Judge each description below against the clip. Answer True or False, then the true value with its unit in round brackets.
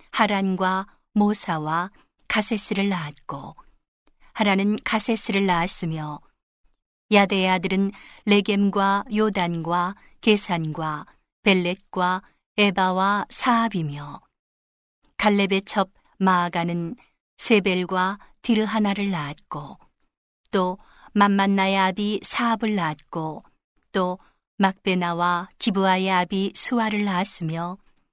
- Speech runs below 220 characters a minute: True (210 characters per minute)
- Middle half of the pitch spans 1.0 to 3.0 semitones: True (2.6 semitones)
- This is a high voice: True (195 Hz)